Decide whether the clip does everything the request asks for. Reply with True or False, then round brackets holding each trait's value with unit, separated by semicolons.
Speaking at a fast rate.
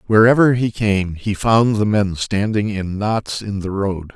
False (190 wpm)